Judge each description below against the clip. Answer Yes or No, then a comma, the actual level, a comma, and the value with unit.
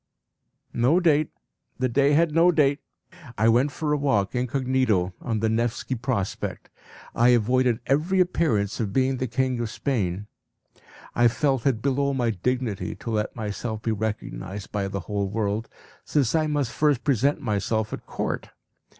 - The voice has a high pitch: No, low, 120 Hz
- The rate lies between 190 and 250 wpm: No, average, 160 wpm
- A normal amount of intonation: Yes, average, 4.4 semitones